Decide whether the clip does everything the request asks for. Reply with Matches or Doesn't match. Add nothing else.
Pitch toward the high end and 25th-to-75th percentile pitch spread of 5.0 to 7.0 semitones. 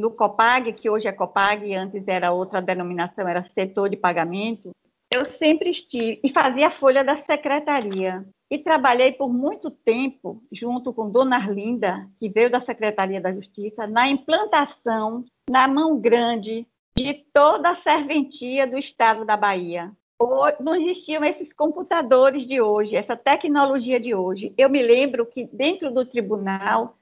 Matches